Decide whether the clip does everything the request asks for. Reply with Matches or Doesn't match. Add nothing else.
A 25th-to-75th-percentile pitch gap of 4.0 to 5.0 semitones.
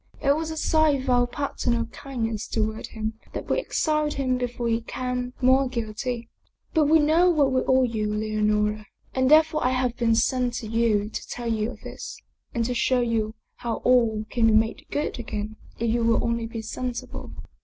Doesn't match